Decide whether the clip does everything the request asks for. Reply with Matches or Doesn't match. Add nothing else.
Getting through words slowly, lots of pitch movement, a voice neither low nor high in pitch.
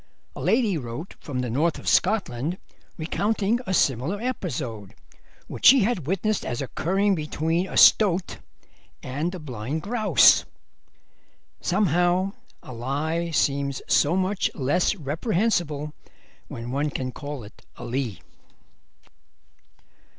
Matches